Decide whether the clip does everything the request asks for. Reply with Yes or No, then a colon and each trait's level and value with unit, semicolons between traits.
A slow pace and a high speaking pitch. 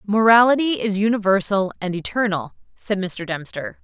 Yes: slow, 125 wpm; high, 205 Hz